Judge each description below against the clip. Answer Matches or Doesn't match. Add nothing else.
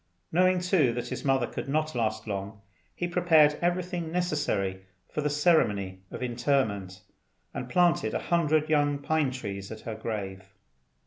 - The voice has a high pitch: Doesn't match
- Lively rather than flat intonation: Matches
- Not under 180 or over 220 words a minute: Doesn't match